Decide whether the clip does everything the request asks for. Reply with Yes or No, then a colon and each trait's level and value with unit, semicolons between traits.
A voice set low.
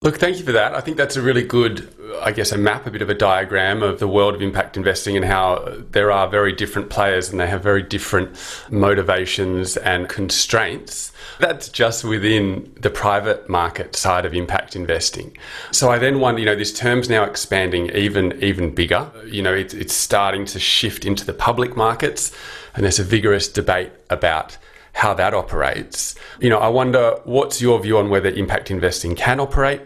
Yes: low, 100 Hz